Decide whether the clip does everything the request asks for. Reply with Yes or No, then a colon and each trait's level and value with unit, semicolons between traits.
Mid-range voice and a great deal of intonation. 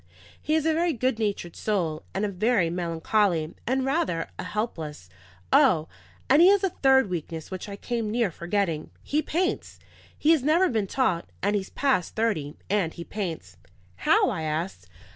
No: high, 205 Hz; wide, 7.9 semitones